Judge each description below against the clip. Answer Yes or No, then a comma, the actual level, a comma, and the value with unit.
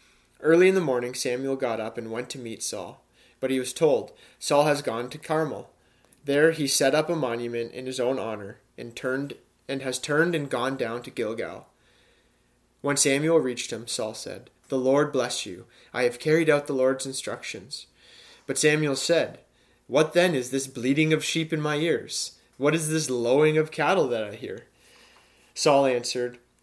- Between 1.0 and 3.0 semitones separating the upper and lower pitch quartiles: No, average, 3.7 semitones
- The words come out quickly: No, average, 185 wpm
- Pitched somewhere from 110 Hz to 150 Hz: Yes, low, 135 Hz